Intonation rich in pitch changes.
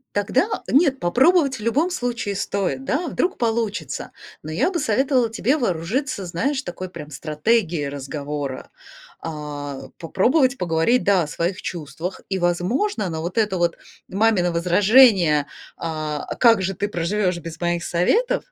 Yes: wide, 6.8 semitones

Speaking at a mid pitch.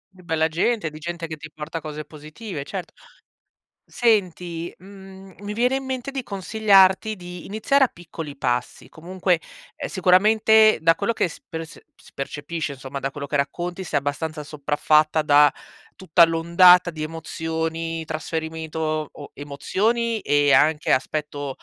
Yes: medium, 165 Hz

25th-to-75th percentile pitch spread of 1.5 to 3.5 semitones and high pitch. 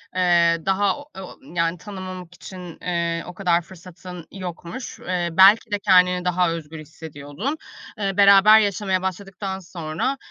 No: narrow, 2.5 semitones; medium, 180 Hz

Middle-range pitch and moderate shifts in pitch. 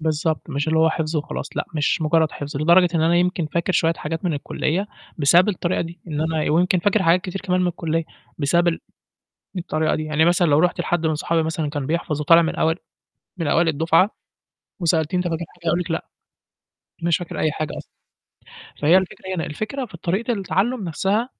No: medium, 165 Hz; narrow, 2.3 semitones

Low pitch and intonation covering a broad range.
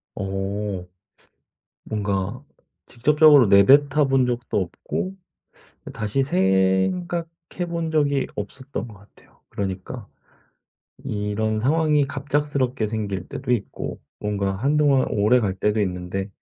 Yes: low, 110 Hz; wide, 6.2 semitones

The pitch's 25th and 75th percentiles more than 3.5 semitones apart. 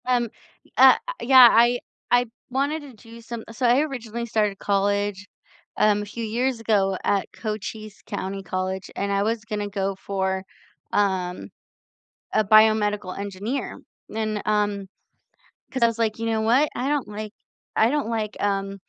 No: average, 2.7 semitones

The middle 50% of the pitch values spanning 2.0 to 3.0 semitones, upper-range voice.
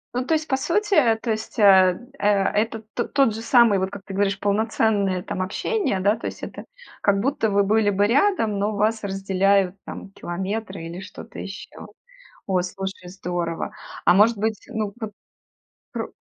Yes: narrow, 2.6 semitones; high, 205 Hz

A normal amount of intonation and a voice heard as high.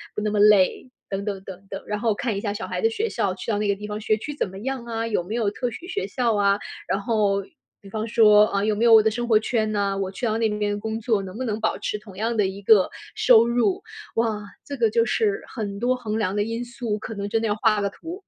No: narrow, 2.3 semitones; high, 215 Hz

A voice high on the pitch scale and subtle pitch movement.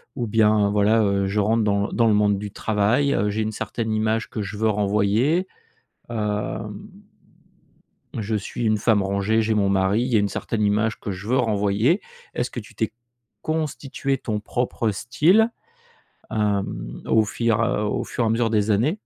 No: low, 110 Hz; narrow, 2.2 semitones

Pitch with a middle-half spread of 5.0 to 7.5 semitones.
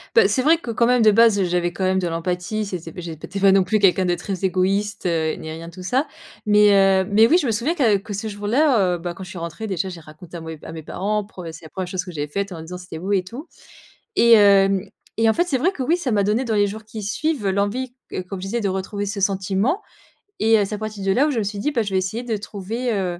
No: average, 3.5 semitones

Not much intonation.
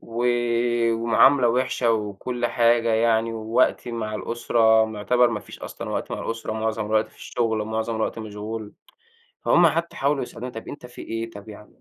Yes: narrow, 1.7 semitones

